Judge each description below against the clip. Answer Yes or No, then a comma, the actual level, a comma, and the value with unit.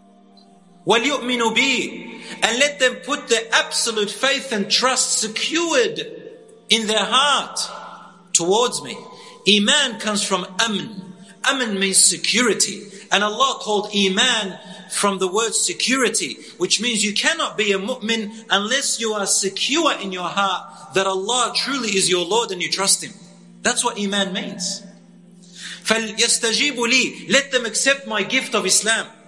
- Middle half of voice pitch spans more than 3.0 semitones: Yes, average, 4.4 semitones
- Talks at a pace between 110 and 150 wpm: Yes, slow, 135 wpm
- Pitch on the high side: Yes, high, 220 Hz